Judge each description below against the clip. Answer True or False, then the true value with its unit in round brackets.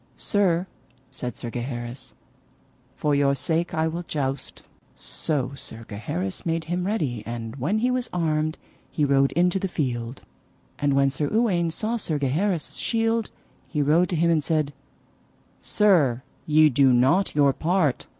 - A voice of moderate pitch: True (150 Hz)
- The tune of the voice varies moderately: True (4.8 semitones)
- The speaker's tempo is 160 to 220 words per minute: False (150 wpm)